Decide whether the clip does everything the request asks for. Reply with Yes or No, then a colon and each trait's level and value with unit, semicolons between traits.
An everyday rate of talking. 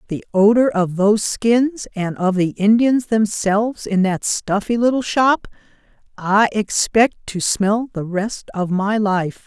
Yes: average, 150 wpm